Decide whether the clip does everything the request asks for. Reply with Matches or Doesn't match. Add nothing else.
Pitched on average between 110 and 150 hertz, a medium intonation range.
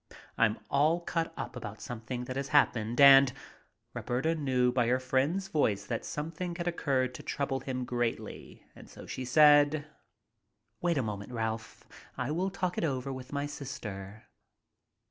Matches